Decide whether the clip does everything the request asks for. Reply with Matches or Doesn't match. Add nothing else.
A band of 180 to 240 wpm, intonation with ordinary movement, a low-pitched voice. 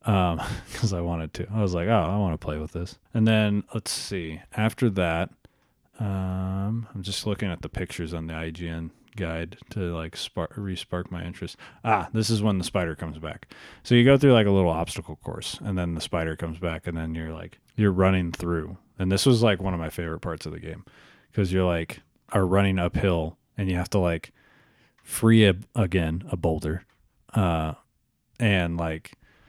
Matches